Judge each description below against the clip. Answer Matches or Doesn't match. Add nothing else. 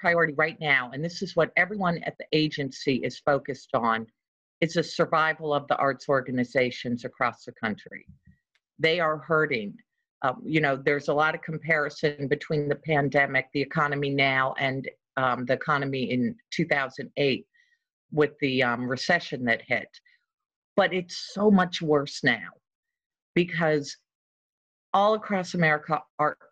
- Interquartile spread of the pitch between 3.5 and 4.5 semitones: Matches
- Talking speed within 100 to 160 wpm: Matches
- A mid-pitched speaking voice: Matches